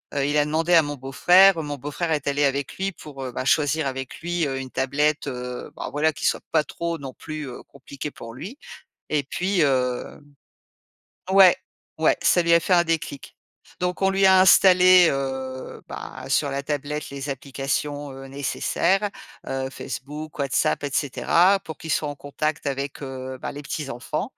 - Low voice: No, medium, 145 Hz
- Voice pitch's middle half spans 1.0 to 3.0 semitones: No, average, 3.5 semitones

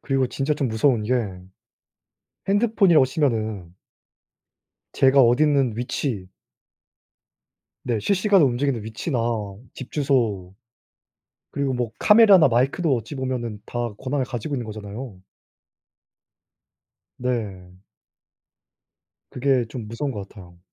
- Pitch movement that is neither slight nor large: Yes, average, 4.3 semitones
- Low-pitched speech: Yes, low, 125 Hz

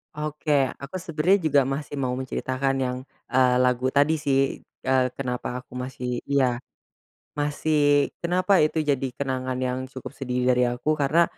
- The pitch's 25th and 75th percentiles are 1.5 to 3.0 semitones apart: Yes, narrow, 2.6 semitones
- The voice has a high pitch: No, low, 135 Hz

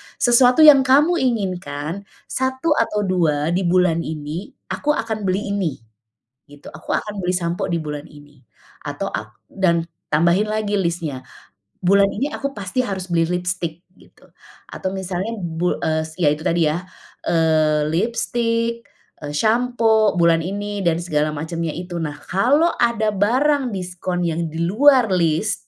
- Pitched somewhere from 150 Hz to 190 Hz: Yes, medium, 185 Hz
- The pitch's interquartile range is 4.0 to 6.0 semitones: Yes, average, 5.0 semitones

